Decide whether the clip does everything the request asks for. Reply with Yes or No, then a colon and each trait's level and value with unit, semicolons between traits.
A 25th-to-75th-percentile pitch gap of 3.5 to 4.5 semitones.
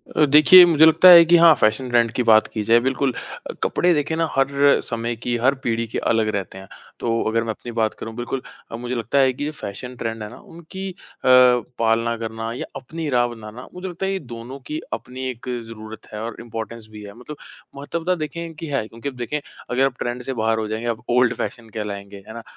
Yes: average, 4.2 semitones